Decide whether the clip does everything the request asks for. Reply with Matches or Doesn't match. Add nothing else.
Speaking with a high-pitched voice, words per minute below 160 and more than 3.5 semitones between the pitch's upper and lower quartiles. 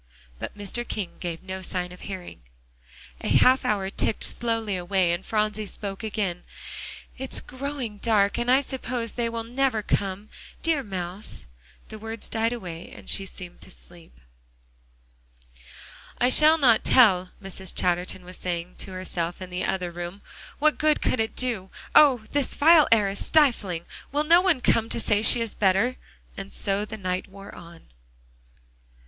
Doesn't match